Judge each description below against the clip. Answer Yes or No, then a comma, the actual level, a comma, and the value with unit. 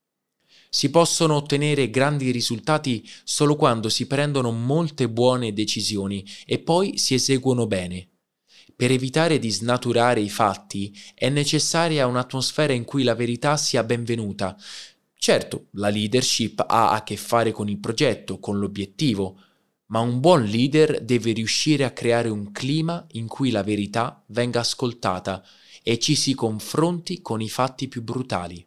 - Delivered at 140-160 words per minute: Yes, average, 145 wpm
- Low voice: Yes, low, 120 Hz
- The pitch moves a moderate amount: Yes, average, 4.7 semitones